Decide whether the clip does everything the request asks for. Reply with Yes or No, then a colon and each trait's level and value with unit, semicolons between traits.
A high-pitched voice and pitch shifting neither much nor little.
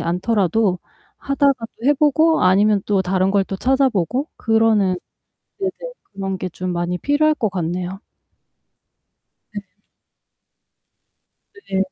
No: high, 200 Hz; wide, 6.1 semitones